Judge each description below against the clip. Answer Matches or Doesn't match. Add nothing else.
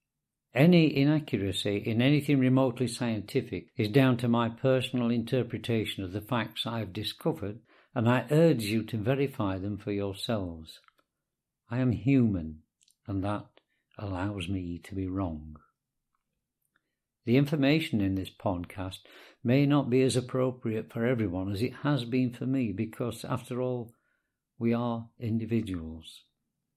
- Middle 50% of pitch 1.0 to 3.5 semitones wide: Doesn't match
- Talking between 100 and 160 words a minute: Matches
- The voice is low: Matches